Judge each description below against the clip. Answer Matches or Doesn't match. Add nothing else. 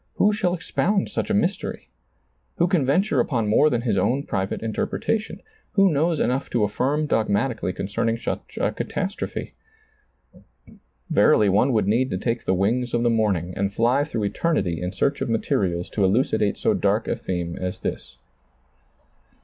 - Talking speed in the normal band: Matches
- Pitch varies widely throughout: Matches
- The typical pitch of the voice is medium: Doesn't match